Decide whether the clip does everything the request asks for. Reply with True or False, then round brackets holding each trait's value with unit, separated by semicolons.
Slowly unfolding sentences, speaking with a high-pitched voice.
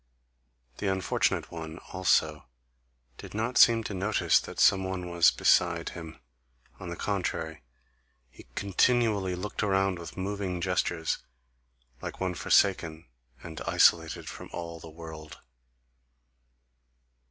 False (120 wpm; 90 Hz)